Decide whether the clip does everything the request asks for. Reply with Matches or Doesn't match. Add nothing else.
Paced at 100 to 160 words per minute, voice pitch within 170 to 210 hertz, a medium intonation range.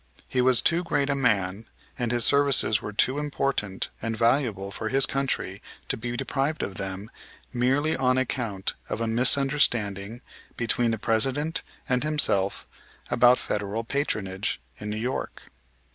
Doesn't match